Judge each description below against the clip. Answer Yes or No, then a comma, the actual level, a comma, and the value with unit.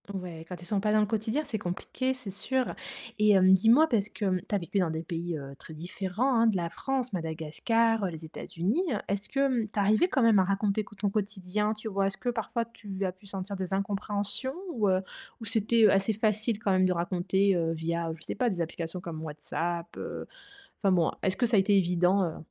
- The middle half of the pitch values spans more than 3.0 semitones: Yes, average, 3.7 semitones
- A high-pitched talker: Yes, high, 195 Hz